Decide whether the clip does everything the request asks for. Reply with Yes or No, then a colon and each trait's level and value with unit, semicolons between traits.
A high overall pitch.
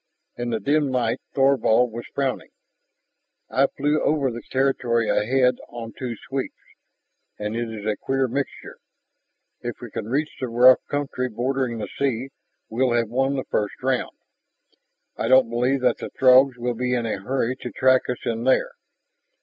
No: low, 125 Hz